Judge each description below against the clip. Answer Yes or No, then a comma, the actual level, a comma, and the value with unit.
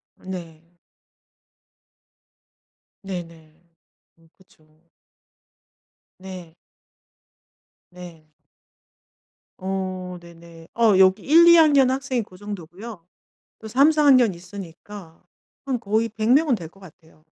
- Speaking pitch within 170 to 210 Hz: Yes, high, 190 Hz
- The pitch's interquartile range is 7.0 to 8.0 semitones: No, average, 5.3 semitones